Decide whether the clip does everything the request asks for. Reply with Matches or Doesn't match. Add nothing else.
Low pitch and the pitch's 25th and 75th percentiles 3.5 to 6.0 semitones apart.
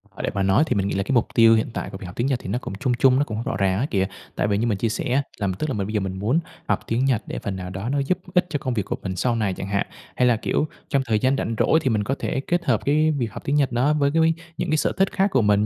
Matches